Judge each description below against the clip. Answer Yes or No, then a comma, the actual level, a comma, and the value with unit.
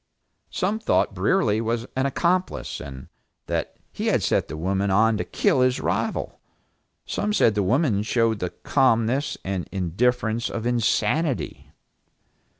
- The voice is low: Yes, low, 115 Hz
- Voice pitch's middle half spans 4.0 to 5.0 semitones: Yes, average, 4.5 semitones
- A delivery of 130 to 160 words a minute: Yes, average, 140 wpm